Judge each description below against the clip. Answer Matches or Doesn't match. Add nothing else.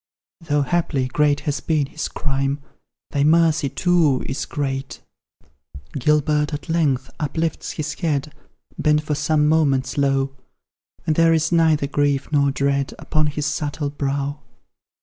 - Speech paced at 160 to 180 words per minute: Doesn't match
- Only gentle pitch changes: Matches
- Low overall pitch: Doesn't match